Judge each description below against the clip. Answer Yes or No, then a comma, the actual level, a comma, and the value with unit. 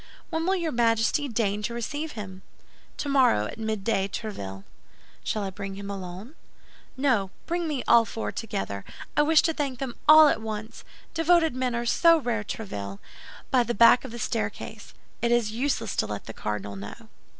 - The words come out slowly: No, average, 170 wpm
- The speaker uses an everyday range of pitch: No, wide, 5.8 semitones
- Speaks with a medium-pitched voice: No, high, 230 Hz